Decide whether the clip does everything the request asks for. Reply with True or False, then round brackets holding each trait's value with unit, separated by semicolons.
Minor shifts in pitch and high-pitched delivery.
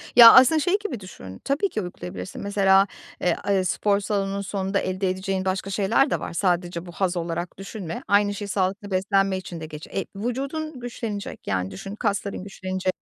True (2.1 semitones; 195 Hz)